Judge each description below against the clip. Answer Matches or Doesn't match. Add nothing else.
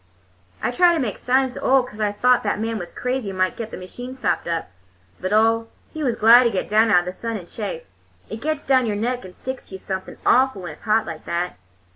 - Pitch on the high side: Matches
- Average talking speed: Doesn't match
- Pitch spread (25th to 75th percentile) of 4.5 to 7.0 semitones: Matches